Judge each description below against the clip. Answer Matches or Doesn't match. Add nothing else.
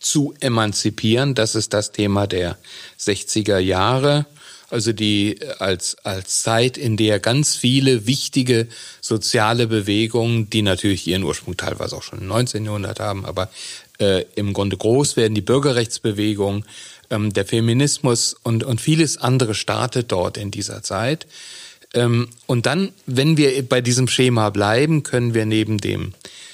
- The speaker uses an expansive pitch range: Doesn't match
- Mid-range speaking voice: Doesn't match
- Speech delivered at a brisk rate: Doesn't match